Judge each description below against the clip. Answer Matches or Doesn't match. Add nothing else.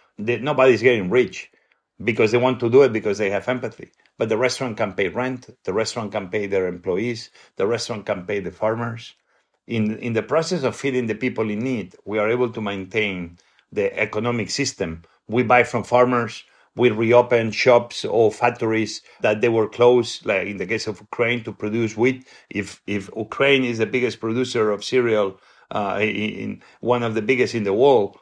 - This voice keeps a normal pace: Matches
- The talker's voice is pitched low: Matches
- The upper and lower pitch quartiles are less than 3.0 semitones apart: Matches